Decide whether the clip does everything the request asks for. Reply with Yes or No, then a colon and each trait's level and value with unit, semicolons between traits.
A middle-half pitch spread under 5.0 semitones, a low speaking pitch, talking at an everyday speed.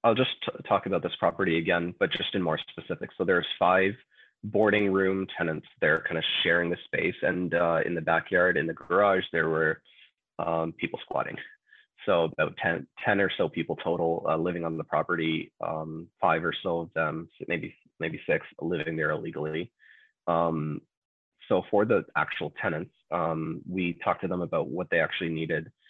Yes: narrow, 2.5 semitones; very low, 85 Hz; average, 185 wpm